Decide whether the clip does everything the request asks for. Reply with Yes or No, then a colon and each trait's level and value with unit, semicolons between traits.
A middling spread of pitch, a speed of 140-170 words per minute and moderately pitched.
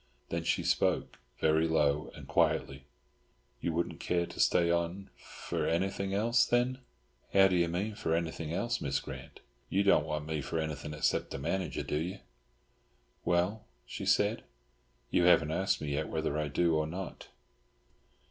No: average, 3.8 semitones; average, 160 wpm; very low, 85 Hz